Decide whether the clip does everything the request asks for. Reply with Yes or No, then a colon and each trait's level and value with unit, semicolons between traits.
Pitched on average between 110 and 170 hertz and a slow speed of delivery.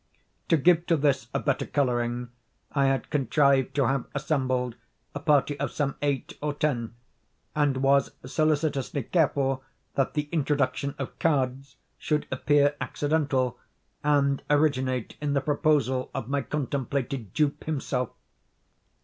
Yes: medium, 140 Hz; slow, 130 wpm